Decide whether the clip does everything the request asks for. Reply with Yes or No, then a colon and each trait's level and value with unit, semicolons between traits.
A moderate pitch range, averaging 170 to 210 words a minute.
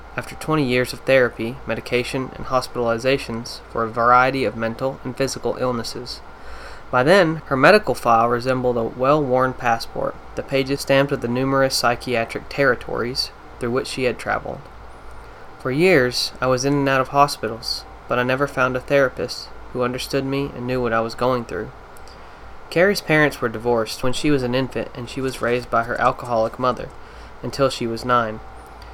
No: narrow, 2.2 semitones; average, 175 wpm